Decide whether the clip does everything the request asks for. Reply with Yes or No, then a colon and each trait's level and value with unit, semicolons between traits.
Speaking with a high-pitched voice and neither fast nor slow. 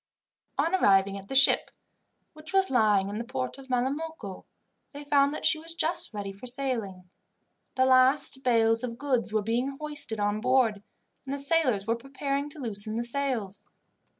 Yes: very high, 255 Hz; average, 175 wpm